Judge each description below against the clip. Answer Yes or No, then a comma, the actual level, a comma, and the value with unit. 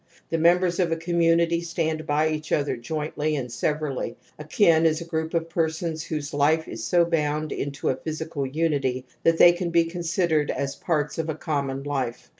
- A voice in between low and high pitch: Yes, medium, 160 Hz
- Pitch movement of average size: No, narrow, 2.3 semitones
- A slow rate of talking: No, average, 190 wpm